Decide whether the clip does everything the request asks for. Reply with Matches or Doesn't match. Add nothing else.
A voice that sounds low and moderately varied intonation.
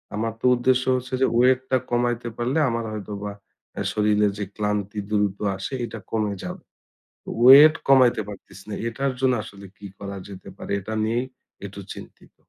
Matches